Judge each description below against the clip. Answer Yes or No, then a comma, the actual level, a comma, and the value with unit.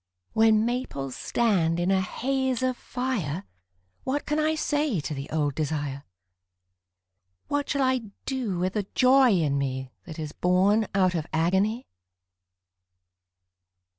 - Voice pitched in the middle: No, high, 195 Hz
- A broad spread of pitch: Yes, wide, 8.3 semitones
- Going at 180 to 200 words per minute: No, slow, 135 wpm